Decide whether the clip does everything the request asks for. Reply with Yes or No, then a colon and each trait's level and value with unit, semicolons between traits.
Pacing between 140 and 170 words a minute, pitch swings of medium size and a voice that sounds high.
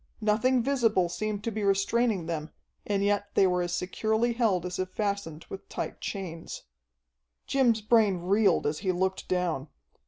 Yes: average, 160 wpm; average, 3.4 semitones; high, 200 Hz